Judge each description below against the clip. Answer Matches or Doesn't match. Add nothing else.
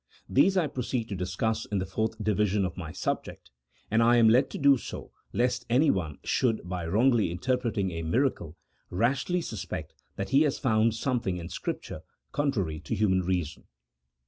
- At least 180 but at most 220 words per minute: Doesn't match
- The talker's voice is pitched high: Doesn't match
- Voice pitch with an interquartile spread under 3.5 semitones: Doesn't match